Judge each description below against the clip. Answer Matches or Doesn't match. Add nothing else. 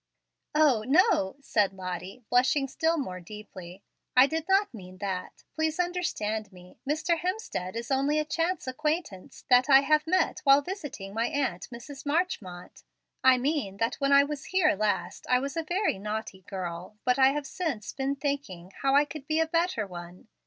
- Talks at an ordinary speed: Matches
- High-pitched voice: Matches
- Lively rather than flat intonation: Matches